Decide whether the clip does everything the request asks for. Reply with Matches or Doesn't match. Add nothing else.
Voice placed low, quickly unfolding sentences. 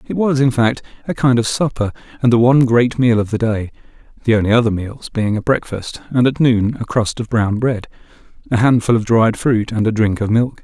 Matches